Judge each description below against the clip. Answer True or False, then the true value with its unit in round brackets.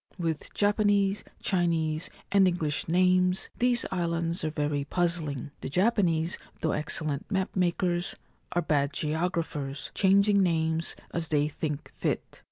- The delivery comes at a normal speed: False (125 wpm)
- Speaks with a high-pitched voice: False (170 Hz)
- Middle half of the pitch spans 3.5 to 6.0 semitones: False (3.1 semitones)